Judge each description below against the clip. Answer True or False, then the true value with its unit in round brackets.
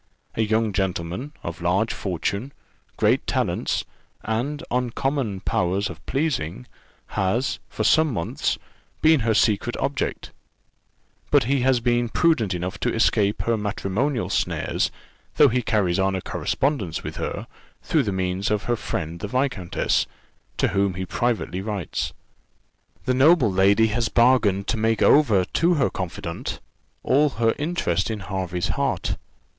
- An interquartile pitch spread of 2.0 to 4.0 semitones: False (5.2 semitones)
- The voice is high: False (110 Hz)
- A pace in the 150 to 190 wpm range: False (140 wpm)